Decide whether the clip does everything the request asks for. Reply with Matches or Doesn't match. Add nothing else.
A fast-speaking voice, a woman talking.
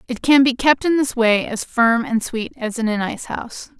Matches